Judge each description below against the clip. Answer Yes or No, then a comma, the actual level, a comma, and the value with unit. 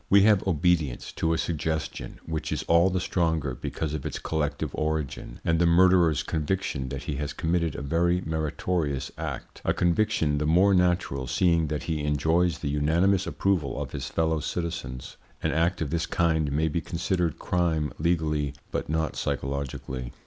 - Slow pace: No, average, 170 wpm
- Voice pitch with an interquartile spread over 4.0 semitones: No, average, 2.9 semitones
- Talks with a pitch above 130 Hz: No, very low, 80 Hz